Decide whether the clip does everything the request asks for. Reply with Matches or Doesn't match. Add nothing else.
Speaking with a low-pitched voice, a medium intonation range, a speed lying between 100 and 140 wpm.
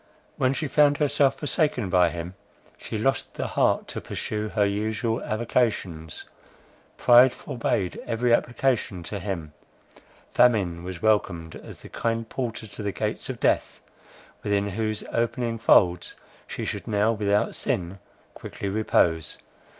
Matches